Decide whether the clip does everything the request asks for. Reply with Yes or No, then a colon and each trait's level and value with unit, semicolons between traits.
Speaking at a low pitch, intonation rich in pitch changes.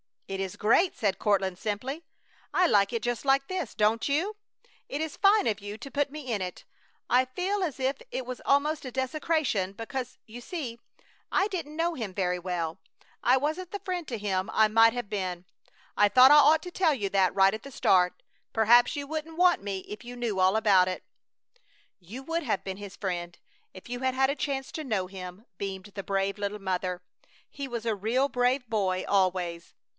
No: high, 230 Hz; wide, 6.3 semitones